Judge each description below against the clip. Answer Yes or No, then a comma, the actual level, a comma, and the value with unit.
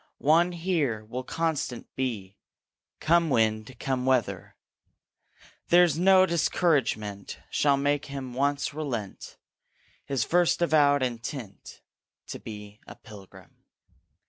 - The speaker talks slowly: Yes, slow, 105 wpm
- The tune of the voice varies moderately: No, wide, 5.9 semitones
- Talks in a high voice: No, low, 135 Hz